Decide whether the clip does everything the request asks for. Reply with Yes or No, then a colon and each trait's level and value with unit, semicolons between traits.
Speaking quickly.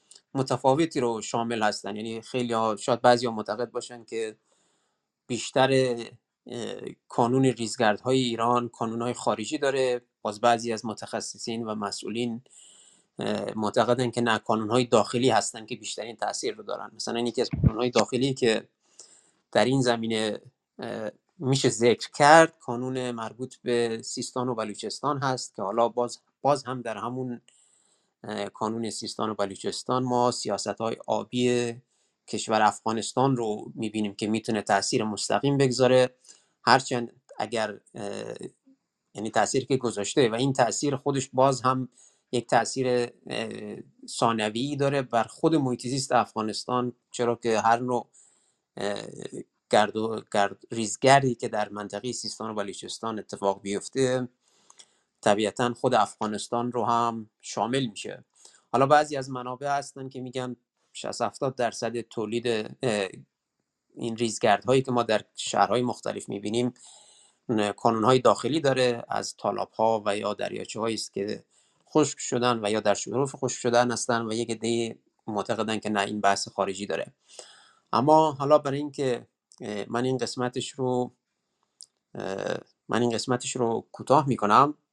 No: average, 135 wpm